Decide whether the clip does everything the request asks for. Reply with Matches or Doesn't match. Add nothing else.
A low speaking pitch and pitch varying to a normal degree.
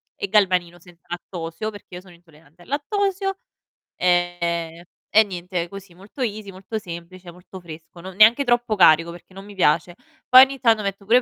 Doesn't match